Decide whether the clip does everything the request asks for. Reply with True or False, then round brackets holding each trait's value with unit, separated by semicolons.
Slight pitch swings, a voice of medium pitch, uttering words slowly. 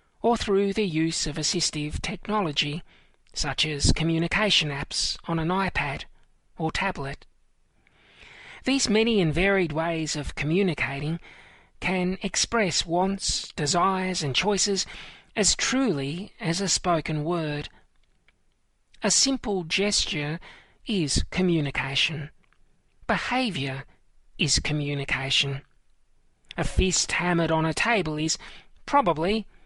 False (4.7 semitones; 170 Hz; 105 wpm)